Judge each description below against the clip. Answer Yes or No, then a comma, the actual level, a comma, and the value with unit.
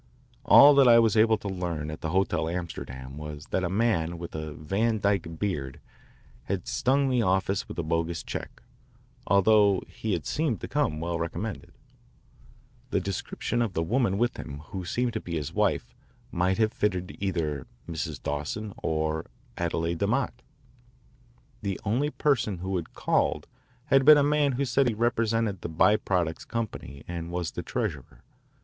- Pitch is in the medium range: No, very low, 95 Hz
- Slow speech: No, average, 170 wpm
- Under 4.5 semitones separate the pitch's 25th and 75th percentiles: No, wide, 5.5 semitones